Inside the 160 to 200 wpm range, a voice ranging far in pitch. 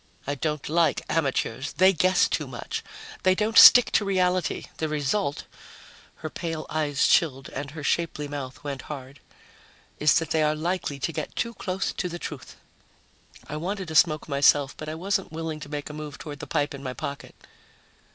No: average, 190 wpm; average, 3.2 semitones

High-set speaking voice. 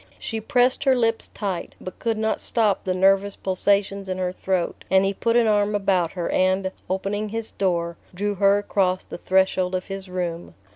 Yes: high, 195 Hz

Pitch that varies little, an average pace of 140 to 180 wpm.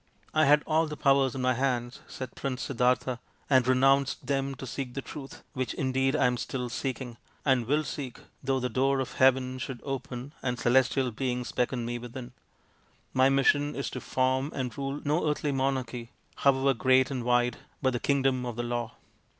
No: narrow, 1.7 semitones; average, 190 wpm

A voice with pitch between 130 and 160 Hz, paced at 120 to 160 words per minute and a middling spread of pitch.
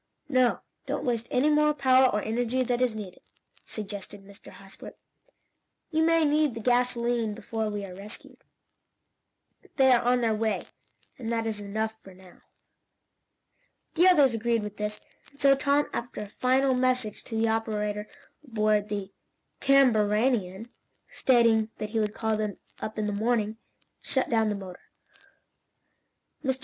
No: high, 225 Hz; average, 150 wpm; average, 3.3 semitones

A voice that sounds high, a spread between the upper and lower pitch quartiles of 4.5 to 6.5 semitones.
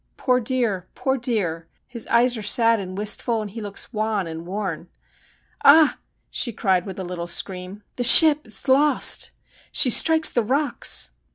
Yes: high, 220 Hz; average, 5.0 semitones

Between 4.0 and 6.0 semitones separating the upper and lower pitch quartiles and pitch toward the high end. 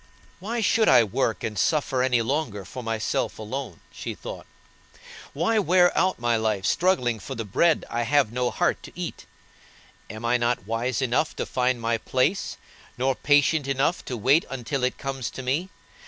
No: average, 4.3 semitones; low, 130 Hz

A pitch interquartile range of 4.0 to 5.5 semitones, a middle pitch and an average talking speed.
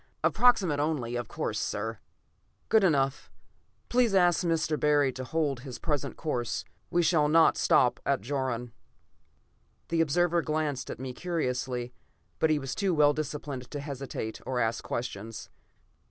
Yes: average, 4.4 semitones; medium, 145 Hz; average, 150 wpm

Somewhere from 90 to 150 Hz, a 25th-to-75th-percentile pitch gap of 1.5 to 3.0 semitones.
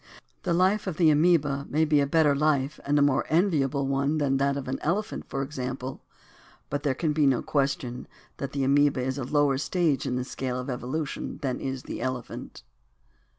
Yes: medium, 140 Hz; narrow, 2.5 semitones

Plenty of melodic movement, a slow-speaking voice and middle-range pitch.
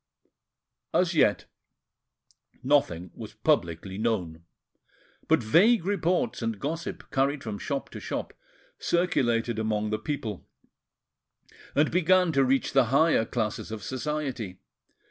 No: wide, 6.1 semitones; slow, 115 wpm; low, 130 Hz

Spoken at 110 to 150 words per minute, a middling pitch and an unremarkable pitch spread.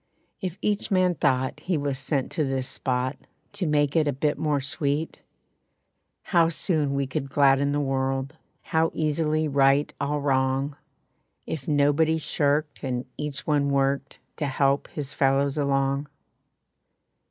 No: average, 140 wpm; medium, 145 Hz; narrow, 1.9 semitones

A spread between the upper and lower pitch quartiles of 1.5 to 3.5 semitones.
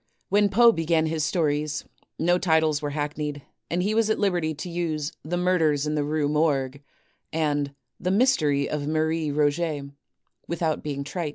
Yes: average, 2.9 semitones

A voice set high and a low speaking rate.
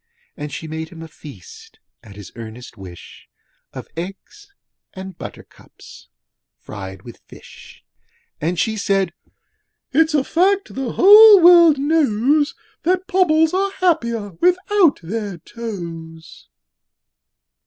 Yes: high, 230 Hz; slow, 115 wpm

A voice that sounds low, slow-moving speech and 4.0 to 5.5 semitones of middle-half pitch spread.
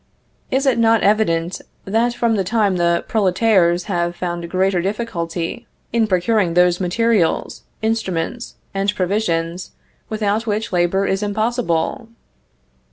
No: high, 195 Hz; slow, 120 wpm; average, 4.3 semitones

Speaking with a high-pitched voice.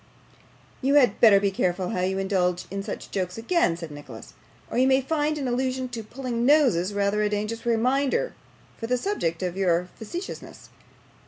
Yes: high, 225 Hz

